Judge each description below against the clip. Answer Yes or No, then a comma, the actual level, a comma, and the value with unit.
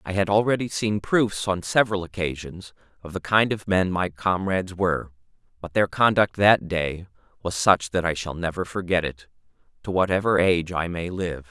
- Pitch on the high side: No, very low, 90 Hz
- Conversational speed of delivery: Yes, average, 180 wpm